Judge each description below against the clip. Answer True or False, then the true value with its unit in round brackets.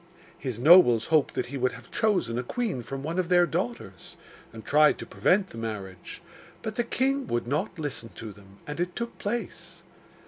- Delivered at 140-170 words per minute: False (195 wpm)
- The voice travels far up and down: True (8.3 semitones)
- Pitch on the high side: False (150 Hz)